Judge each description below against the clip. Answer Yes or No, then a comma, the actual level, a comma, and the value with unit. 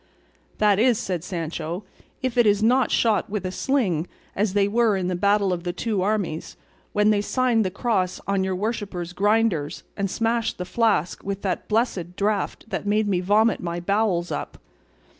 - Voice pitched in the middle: No, high, 200 Hz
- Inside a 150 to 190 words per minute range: Yes, average, 180 wpm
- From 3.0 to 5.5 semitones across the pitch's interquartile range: Yes, average, 3.3 semitones